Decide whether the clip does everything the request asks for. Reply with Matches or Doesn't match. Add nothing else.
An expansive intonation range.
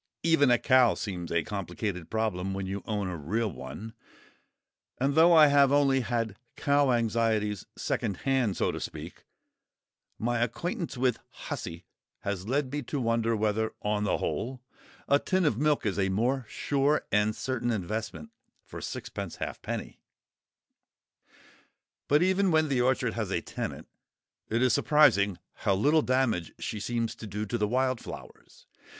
Doesn't match